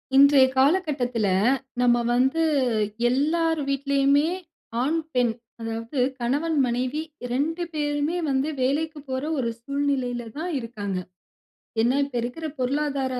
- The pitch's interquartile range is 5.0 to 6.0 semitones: No, average, 3.3 semitones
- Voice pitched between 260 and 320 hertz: Yes, very high, 275 Hz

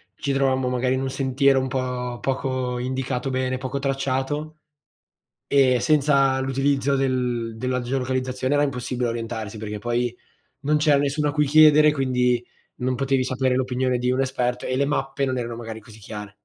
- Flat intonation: Yes, narrow, 1.7 semitones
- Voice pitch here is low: Yes, low, 130 Hz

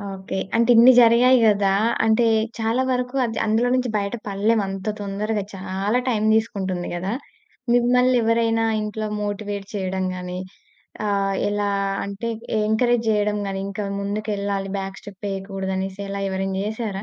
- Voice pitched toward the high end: Yes, high, 205 Hz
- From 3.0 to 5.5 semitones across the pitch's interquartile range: No, narrow, 2.6 semitones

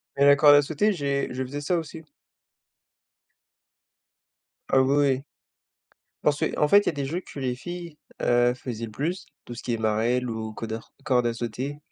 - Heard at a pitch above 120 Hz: Yes, low, 135 Hz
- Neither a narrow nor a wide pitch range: Yes, average, 3.4 semitones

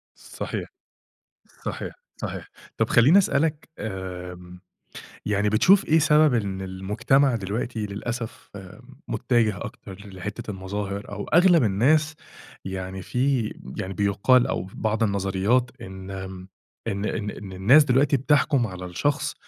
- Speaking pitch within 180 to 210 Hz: No, low, 105 Hz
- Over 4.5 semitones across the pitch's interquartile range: Yes, average, 5.1 semitones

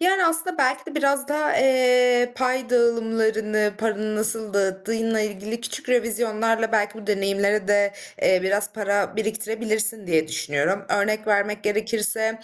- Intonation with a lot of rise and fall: No, narrow, 2.6 semitones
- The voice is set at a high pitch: Yes, high, 220 Hz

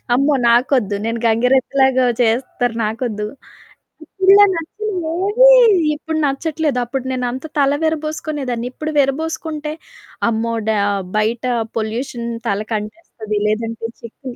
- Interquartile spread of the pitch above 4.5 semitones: Yes, average, 5.2 semitones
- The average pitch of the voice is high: Yes, very high, 260 Hz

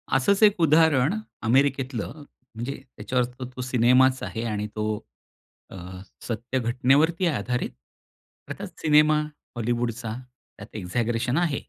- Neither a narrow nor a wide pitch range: Yes, average, 3.5 semitones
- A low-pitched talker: Yes, low, 125 Hz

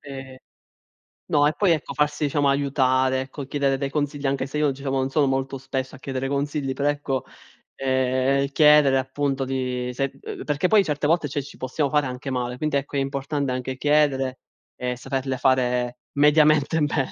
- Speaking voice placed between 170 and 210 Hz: No, low, 135 Hz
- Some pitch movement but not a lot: No, narrow, 1.8 semitones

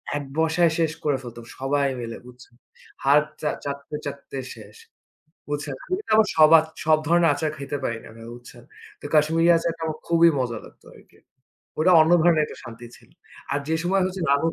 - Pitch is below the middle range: No, medium, 150 Hz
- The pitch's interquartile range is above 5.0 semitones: No, average, 3.0 semitones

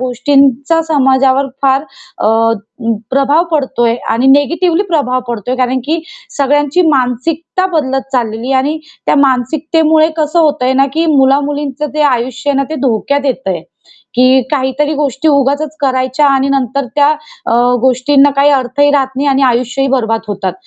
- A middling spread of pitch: No, narrow, 2.3 semitones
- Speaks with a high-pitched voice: Yes, very high, 275 Hz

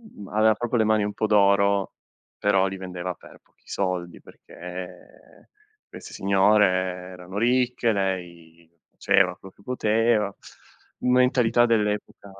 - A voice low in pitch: Yes, low, 100 Hz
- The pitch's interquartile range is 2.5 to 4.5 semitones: Yes, average, 2.9 semitones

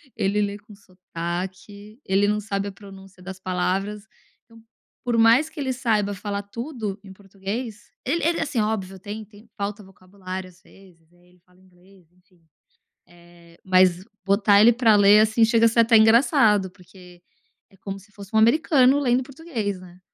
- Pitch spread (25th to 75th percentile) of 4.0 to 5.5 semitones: No, average, 3.2 semitones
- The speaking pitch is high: Yes, high, 200 Hz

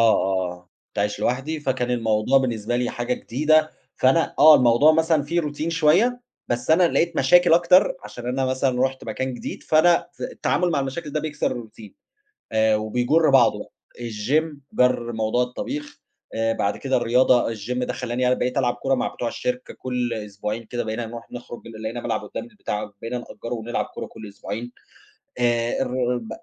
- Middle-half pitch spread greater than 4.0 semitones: Yes, average, 4.4 semitones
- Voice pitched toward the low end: Yes, low, 125 Hz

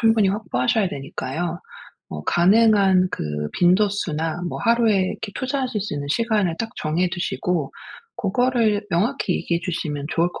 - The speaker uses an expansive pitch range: No, average, 4.6 semitones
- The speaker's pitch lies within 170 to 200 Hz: Yes, high, 190 Hz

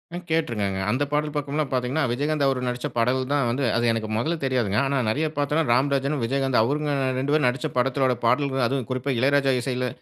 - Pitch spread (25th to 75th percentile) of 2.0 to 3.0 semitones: Yes, average, 2.7 semitones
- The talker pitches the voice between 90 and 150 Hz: Yes, low, 135 Hz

